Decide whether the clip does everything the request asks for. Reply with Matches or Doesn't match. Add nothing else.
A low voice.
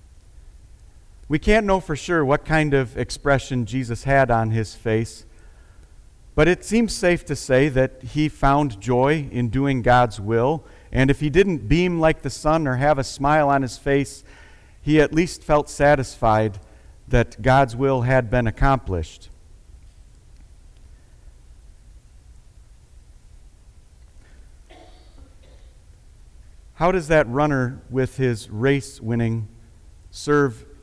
Matches